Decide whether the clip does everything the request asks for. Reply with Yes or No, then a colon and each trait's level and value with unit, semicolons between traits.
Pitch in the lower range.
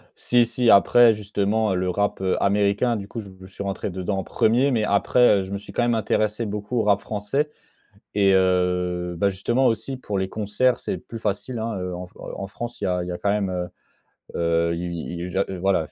Yes: low, 100 Hz